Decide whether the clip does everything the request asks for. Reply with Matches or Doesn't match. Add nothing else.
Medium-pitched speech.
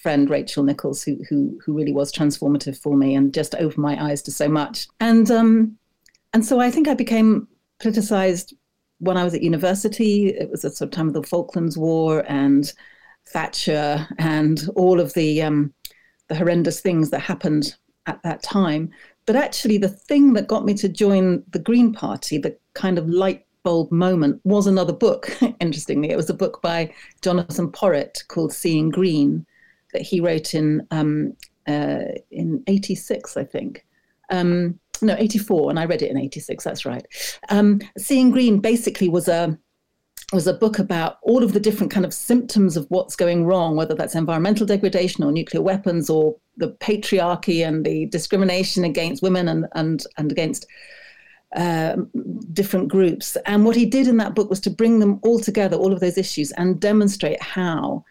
Matches